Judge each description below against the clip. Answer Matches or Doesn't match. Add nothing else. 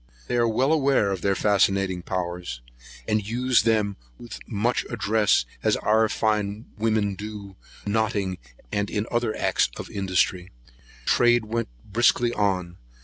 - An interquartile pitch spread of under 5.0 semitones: Matches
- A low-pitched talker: Matches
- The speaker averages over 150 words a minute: Doesn't match